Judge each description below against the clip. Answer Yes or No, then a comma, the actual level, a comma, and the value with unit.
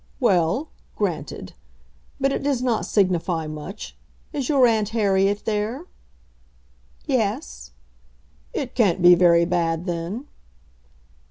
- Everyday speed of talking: No, slow, 105 wpm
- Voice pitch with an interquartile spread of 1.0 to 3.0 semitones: No, wide, 5.6 semitones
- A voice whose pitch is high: Yes, high, 195 Hz